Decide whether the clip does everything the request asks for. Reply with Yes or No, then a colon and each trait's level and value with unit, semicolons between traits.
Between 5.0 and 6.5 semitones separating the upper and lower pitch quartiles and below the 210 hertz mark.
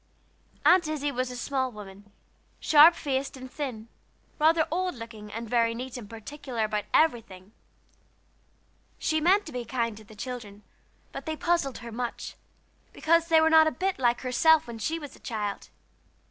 No: wide, 5.5 semitones; very high, 255 Hz